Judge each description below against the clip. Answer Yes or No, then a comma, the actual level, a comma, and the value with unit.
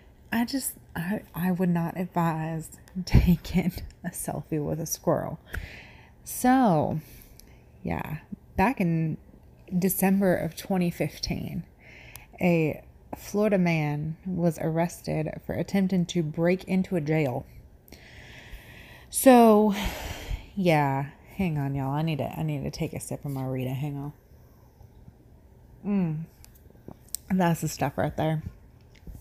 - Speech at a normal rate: No, slow, 115 wpm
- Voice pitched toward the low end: No, medium, 165 Hz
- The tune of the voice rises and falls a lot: No, average, 3.6 semitones